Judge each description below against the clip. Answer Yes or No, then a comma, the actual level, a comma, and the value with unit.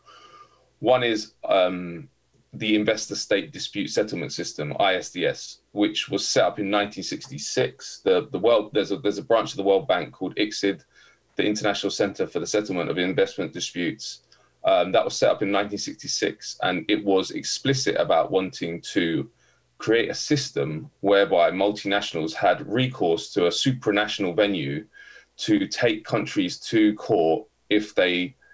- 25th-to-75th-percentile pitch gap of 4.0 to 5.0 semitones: Yes, average, 4.4 semitones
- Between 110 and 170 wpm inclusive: Yes, average, 145 wpm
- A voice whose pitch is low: Yes, low, 105 Hz